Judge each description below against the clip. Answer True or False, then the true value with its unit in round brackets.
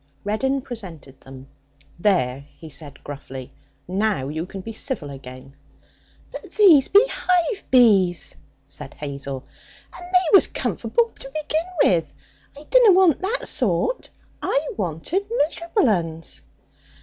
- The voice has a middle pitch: False (205 Hz)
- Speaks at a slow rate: True (125 wpm)